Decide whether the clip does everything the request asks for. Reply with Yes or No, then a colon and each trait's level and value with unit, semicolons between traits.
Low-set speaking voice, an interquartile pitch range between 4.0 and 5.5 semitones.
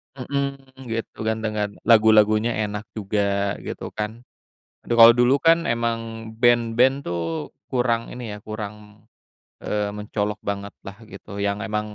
No: low, 110 Hz; narrow, 2.5 semitones